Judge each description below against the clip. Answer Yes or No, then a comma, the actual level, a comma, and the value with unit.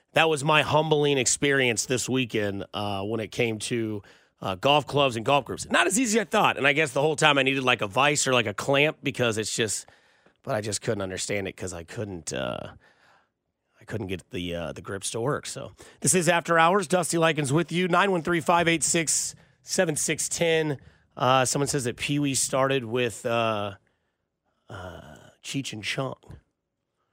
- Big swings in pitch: Yes, wide, 5.7 semitones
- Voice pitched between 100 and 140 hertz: Yes, low, 135 Hz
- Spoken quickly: No, average, 190 wpm